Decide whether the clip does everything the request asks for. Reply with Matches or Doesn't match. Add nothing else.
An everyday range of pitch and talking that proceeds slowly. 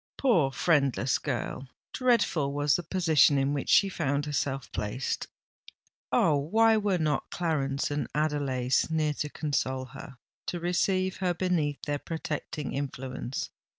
Matches